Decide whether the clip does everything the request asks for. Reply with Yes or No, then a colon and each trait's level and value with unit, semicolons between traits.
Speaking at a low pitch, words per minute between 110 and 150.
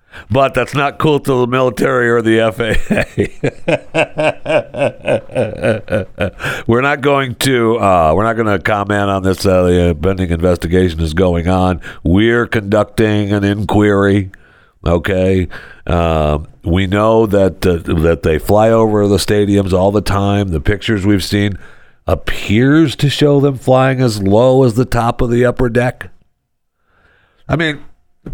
Yes: low, 105 Hz; average, 145 wpm